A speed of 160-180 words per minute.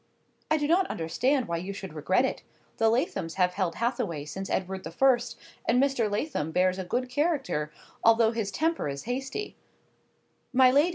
Yes: average, 175 wpm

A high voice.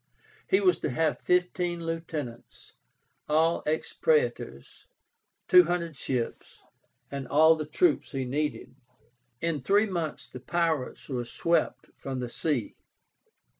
No: medium, 160 Hz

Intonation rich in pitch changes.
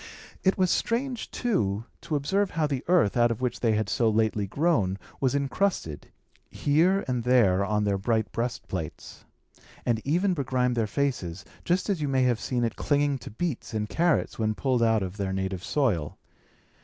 Yes: wide, 5.9 semitones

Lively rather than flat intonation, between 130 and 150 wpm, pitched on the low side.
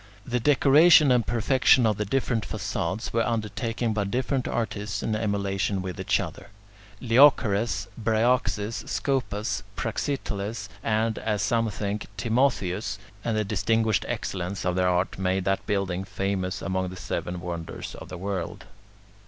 No: average, 3.2 semitones; average, 140 wpm; low, 105 Hz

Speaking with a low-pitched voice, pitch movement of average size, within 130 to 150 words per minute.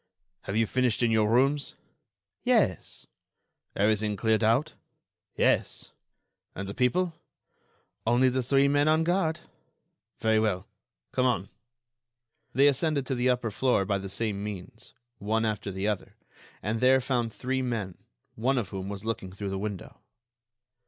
Yes: low, 115 Hz; average, 4.1 semitones; average, 145 wpm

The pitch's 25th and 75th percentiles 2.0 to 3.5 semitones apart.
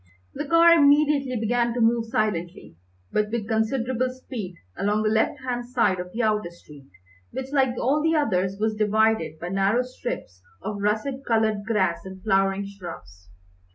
No: average, 4.5 semitones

